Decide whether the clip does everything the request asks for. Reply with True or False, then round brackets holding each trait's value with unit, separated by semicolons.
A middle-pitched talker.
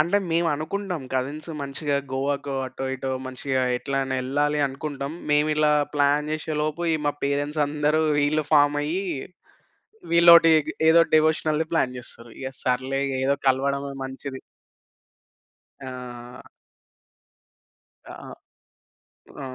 True (145 Hz)